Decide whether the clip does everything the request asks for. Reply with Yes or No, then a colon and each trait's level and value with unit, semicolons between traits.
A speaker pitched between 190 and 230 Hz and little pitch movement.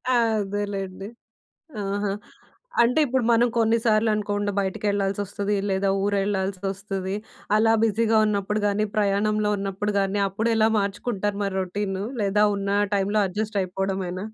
Yes: high, 205 Hz; narrow, 1.5 semitones